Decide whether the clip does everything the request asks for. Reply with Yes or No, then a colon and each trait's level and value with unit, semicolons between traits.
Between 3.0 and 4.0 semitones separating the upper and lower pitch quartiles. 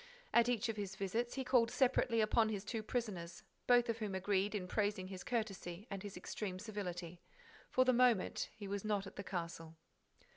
Yes: average, 3.5 semitones